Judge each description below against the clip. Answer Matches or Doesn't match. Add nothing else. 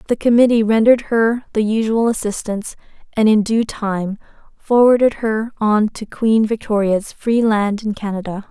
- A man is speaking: Doesn't match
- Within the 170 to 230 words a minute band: Doesn't match